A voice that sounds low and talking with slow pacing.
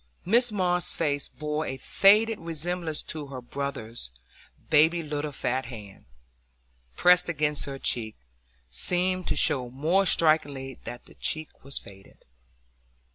No: medium, 150 Hz; slow, 130 wpm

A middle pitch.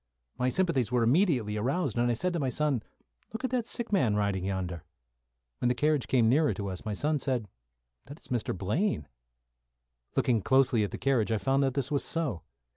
No: low, 125 Hz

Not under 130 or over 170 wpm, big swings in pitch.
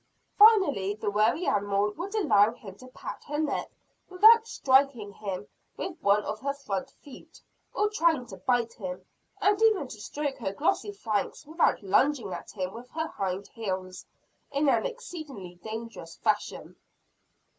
Yes: average, 155 wpm; wide, 7.6 semitones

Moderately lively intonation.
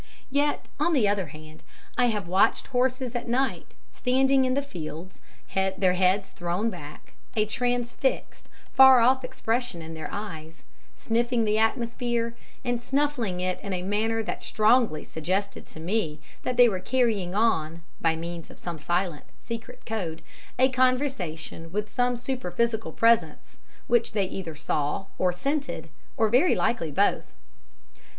No: wide, 5.7 semitones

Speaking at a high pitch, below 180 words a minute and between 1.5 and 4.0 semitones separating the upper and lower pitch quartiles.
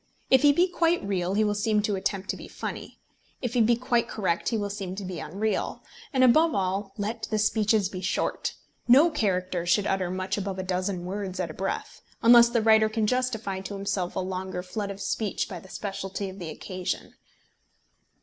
No: high, 200 Hz; fast, 205 wpm; average, 3.0 semitones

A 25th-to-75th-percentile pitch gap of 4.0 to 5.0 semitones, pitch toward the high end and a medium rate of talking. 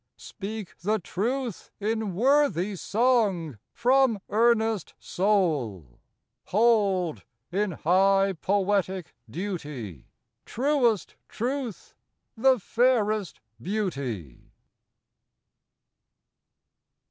No: average, 4.4 semitones; high, 205 Hz; slow, 65 wpm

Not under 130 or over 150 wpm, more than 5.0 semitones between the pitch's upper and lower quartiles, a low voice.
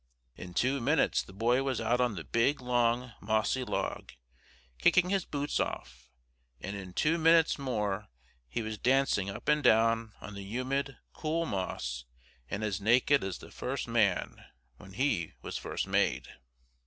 No: average, 160 wpm; wide, 5.5 semitones; low, 115 Hz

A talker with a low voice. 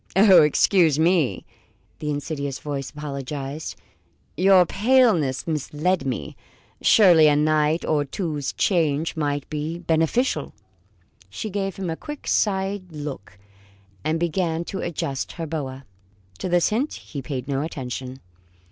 No: medium, 155 Hz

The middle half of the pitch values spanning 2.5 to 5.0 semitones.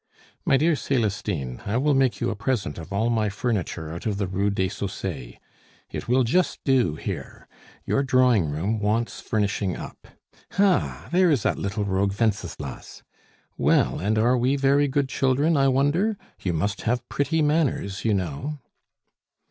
No: wide, 5.6 semitones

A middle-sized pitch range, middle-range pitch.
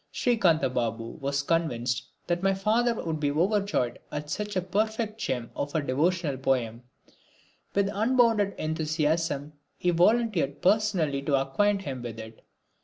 No: wide, 6.8 semitones; medium, 160 Hz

